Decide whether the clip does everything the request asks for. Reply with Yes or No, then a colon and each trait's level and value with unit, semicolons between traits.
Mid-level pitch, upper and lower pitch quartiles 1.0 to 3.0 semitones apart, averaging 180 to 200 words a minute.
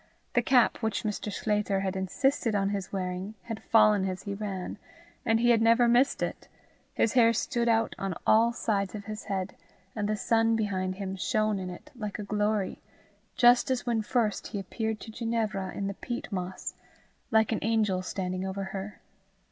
No: high, 210 Hz; average, 2.7 semitones; average, 185 wpm